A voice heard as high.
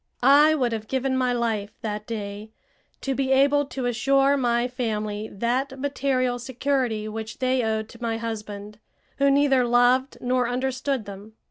Yes: high, 245 Hz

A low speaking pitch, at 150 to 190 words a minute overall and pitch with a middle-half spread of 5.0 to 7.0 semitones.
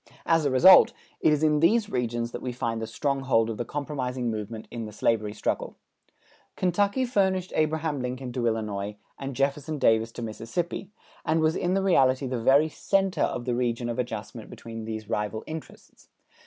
Yes: low, 130 Hz; average, 175 wpm; wide, 5.6 semitones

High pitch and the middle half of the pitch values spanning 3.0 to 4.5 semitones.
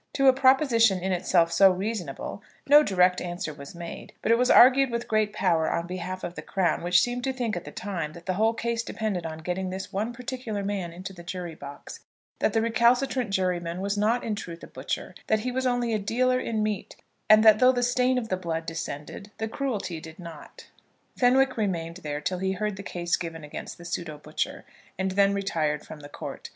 No: high, 195 Hz; average, 5.1 semitones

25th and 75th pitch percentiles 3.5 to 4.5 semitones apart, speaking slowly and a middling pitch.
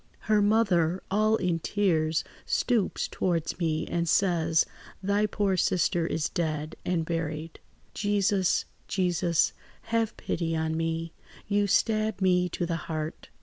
Yes: average, 3.8 semitones; slow, 130 wpm; medium, 175 Hz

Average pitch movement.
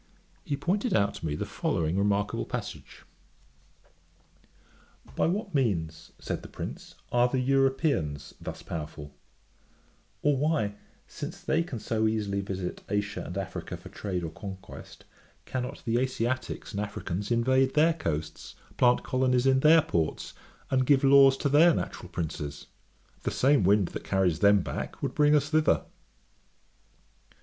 No: wide, 6.3 semitones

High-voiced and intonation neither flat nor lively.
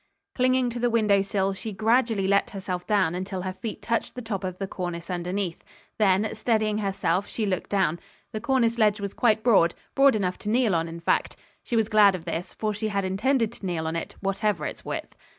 Yes: high, 200 Hz; average, 3.2 semitones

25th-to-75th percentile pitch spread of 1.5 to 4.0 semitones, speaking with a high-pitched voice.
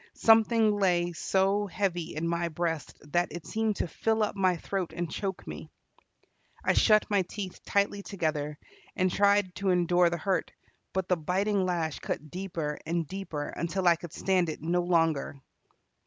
No: average, 2.9 semitones; medium, 180 Hz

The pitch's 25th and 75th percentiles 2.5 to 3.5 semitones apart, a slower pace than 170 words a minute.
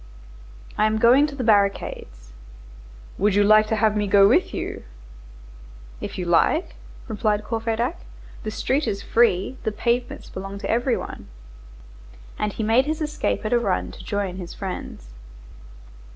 Yes: average, 3.2 semitones; average, 155 wpm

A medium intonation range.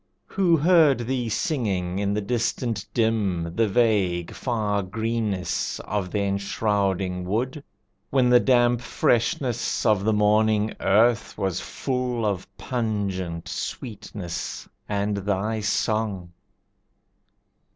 Yes: average, 3.4 semitones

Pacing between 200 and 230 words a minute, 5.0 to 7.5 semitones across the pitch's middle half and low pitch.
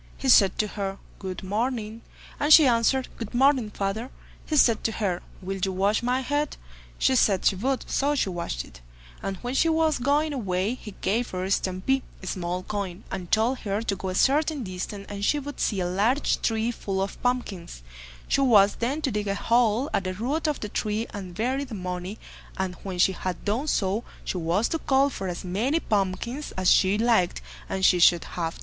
No: fast, 205 wpm; average, 5.3 semitones; high, 215 Hz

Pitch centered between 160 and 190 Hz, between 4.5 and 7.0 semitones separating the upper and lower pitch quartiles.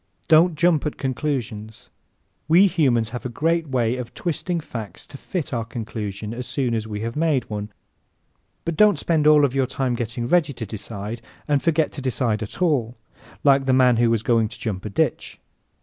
No: low, 125 Hz; average, 5.1 semitones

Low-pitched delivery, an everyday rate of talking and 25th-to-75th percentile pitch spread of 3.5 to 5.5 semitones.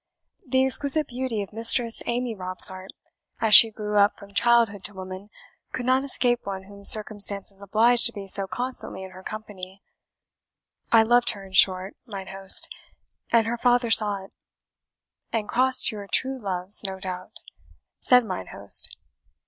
No: high, 210 Hz; average, 155 wpm; average, 3.8 semitones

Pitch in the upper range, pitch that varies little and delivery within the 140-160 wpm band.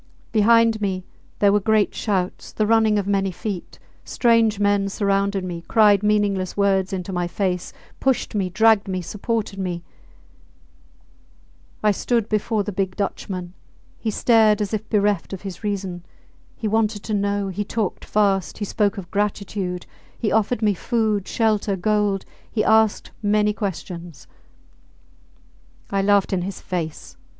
Yes: high, 205 Hz; narrow, 2.0 semitones; average, 145 wpm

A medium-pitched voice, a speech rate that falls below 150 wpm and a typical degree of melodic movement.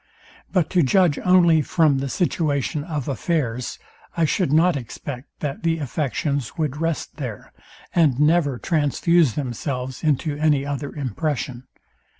Yes: medium, 150 Hz; slow, 135 wpm; average, 3.3 semitones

